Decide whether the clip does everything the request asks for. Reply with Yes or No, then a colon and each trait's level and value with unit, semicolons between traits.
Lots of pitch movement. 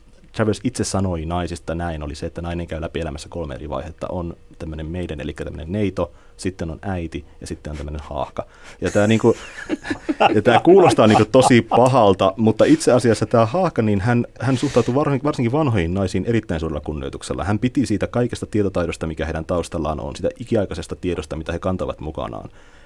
Yes: wide, 5.8 semitones